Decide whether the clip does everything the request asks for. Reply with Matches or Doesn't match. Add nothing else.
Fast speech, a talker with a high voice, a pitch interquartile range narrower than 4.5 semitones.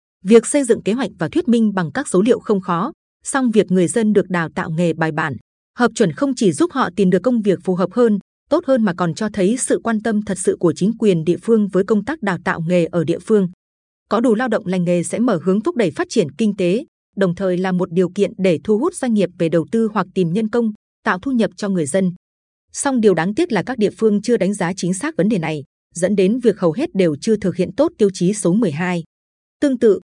Matches